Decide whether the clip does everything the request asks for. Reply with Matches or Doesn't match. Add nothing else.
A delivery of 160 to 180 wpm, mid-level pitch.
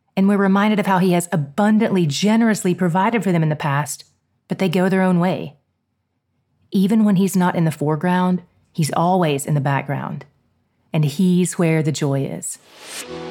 Matches